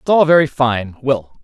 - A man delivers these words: Yes, male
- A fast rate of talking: No, average, 165 wpm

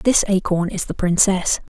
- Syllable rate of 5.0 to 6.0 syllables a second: No, 4.7 syllables/s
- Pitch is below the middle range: No, high, 190 Hz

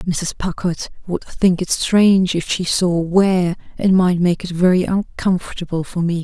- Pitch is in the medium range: Yes, medium, 180 Hz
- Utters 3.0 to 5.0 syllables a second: Yes, 4.7 syllables/s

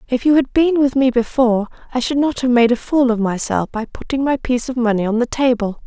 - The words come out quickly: Yes, fast, 255 wpm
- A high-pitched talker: Yes, high, 245 Hz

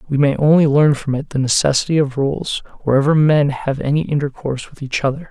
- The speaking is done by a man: Yes, male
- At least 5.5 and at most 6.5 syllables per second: Yes, 5.9 syllables/s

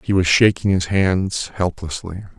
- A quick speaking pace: No, average, 150 wpm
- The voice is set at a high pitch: No, very low, 90 Hz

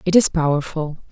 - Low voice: No, medium, 160 Hz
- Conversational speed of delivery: Yes, average, 160 wpm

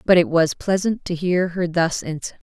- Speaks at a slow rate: No, fast, 215 wpm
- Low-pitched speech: No, medium, 170 Hz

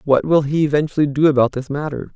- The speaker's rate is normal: No, fast, 225 wpm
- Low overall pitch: No, medium, 145 Hz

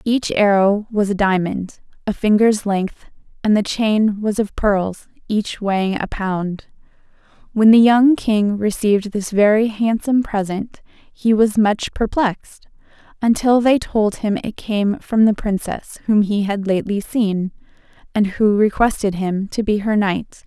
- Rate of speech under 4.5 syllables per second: Yes, 4.1 syllables/s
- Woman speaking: Yes, female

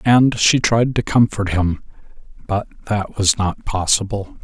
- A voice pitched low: Yes, low, 105 Hz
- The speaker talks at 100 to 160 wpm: Yes, average, 150 wpm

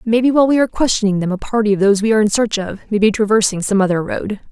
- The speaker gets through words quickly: Yes, fast, 280 wpm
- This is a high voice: Yes, high, 210 Hz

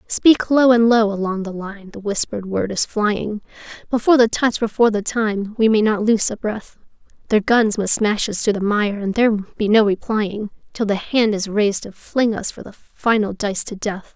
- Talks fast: Yes, fast, 215 wpm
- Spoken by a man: No, female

